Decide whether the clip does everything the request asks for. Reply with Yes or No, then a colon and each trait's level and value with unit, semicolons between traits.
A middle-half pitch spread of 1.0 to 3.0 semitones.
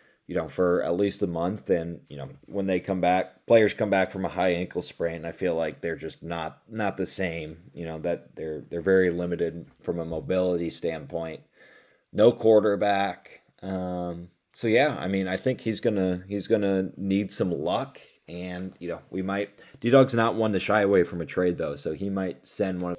Yes: narrow, 2.5 semitones